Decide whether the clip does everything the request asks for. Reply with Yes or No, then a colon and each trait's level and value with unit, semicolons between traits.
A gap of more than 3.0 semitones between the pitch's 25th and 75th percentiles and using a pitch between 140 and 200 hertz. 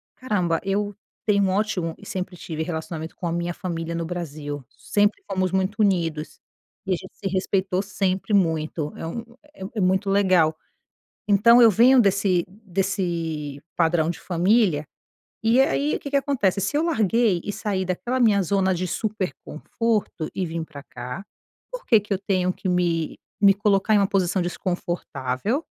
Yes: average, 3.4 semitones; medium, 185 Hz